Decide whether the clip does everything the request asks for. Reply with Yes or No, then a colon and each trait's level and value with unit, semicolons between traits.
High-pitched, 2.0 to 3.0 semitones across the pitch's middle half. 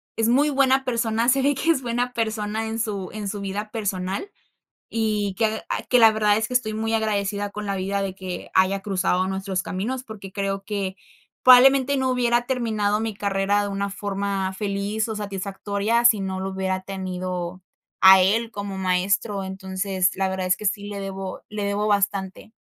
Yes: high, 205 Hz; narrow, 2.5 semitones